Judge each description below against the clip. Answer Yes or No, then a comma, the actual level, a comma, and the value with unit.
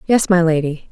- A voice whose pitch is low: No, medium, 175 Hz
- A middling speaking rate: Yes, average, 195 wpm